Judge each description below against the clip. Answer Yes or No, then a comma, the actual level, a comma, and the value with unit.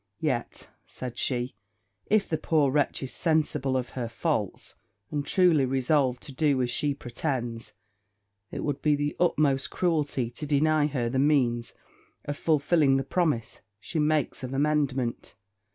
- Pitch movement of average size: Yes, average, 3.1 semitones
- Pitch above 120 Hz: Yes, medium, 140 Hz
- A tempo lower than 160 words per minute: Yes, average, 150 wpm